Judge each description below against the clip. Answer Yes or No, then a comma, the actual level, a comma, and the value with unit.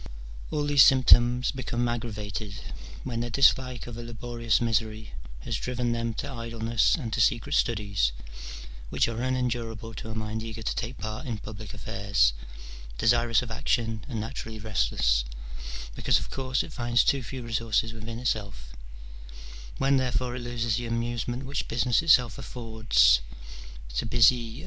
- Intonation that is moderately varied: No, narrow, 1.9 semitones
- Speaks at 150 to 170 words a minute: Yes, average, 155 wpm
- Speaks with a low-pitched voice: Yes, low, 115 Hz